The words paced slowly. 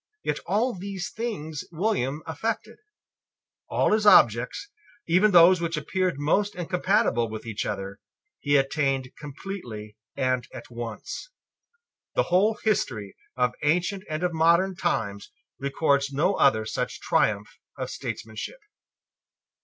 Yes: slow, 120 wpm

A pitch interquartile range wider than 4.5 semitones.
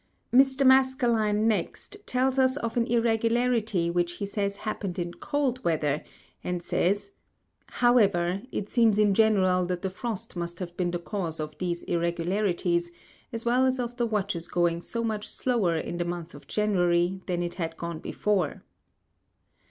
Yes: average, 5.1 semitones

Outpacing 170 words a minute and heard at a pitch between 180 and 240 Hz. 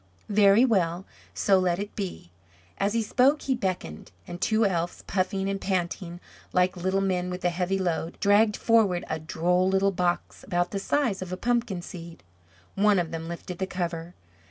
Yes: average, 180 wpm; medium, 185 Hz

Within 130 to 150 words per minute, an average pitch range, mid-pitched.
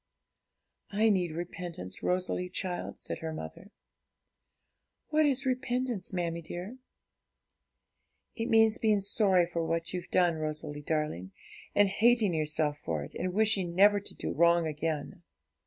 Yes: slow, 135 wpm; average, 4.7 semitones; medium, 180 Hz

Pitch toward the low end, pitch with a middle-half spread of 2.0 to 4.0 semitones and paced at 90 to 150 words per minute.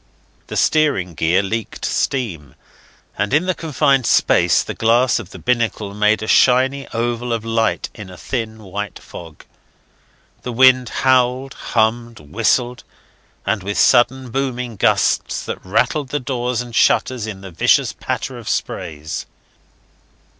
Yes: low, 115 Hz; average, 3.7 semitones; average, 140 wpm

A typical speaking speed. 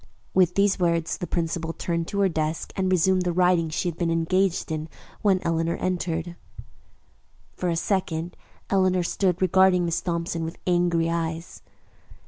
Yes: average, 155 wpm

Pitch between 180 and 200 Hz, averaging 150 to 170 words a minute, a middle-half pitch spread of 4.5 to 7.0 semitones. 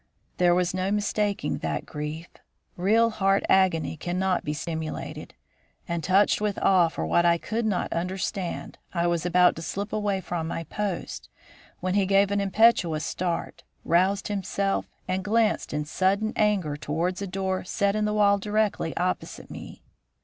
No: medium, 185 Hz; average, 160 wpm; average, 2.9 semitones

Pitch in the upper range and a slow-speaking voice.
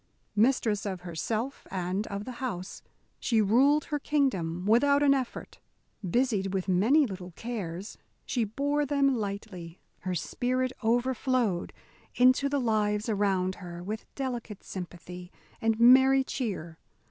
Yes: high, 220 Hz; slow, 130 wpm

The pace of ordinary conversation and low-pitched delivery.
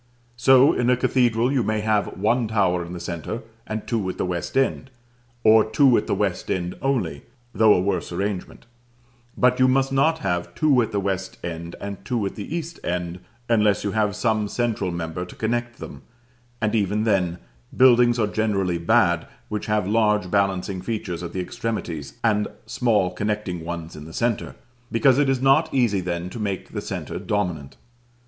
Yes: average, 180 wpm; low, 105 Hz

